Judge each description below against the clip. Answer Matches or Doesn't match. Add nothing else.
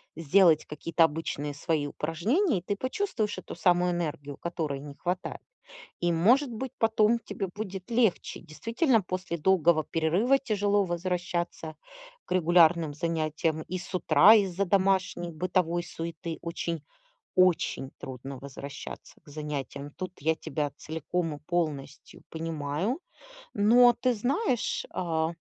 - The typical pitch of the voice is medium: Matches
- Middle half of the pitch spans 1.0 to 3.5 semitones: Doesn't match